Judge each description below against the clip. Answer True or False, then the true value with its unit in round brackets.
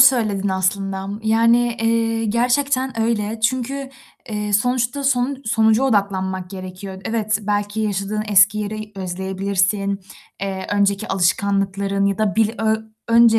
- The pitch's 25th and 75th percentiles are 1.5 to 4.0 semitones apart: True (2.7 semitones)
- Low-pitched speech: False (210 Hz)